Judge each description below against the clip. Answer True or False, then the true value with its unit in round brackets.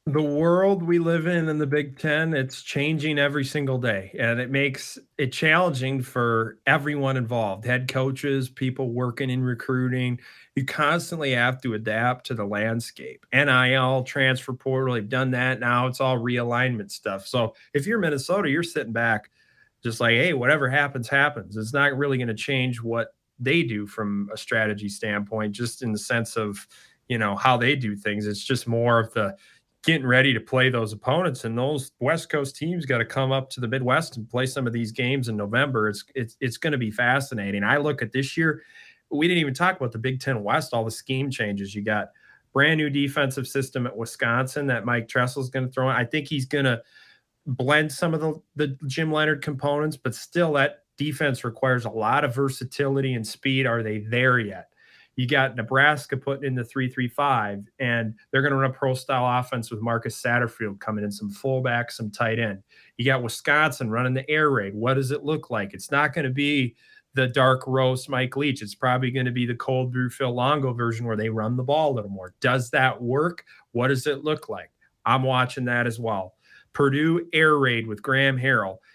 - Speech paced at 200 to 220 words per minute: True (205 wpm)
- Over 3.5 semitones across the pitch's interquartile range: False (3.2 semitones)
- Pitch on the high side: False (130 Hz)